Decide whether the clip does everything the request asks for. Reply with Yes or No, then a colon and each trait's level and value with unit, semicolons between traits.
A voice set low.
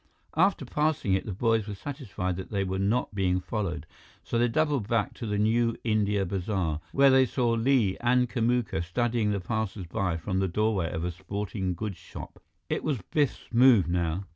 Yes: low, 105 Hz